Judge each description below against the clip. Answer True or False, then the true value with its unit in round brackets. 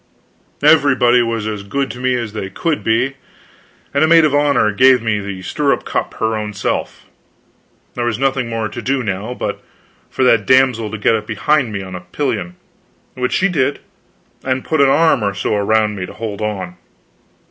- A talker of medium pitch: False (115 Hz)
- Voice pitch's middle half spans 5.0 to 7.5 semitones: False (4.1 semitones)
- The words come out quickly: False (190 wpm)